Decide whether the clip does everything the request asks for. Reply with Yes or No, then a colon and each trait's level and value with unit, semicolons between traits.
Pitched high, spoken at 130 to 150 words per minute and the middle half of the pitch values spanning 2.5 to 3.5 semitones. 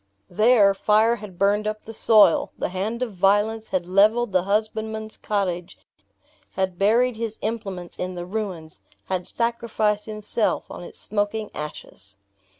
Yes: high, 210 Hz; average, 145 wpm; average, 2.8 semitones